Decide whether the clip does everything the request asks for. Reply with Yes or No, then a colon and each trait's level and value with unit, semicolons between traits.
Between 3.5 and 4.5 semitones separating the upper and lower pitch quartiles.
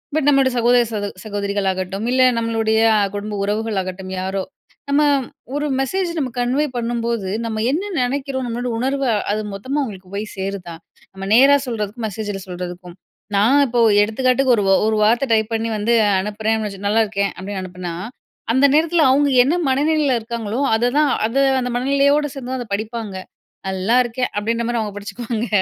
Yes: average, 4.2 semitones